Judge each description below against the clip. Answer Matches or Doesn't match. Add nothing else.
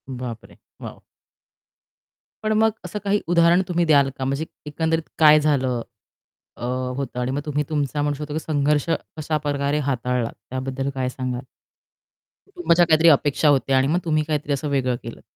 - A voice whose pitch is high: Doesn't match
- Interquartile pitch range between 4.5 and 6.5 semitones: Doesn't match